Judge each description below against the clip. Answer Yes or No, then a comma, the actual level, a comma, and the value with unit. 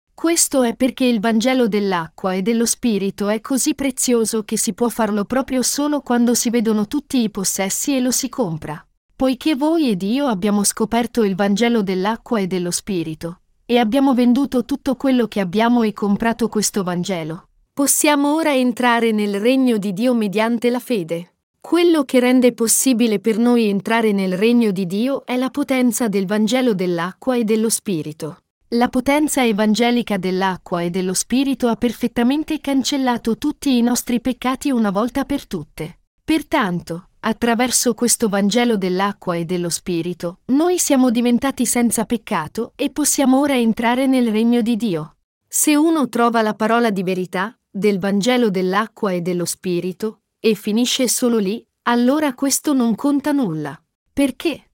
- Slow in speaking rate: No, average, 155 wpm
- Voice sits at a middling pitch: No, high, 235 Hz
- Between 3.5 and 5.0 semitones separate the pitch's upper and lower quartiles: Yes, average, 4.1 semitones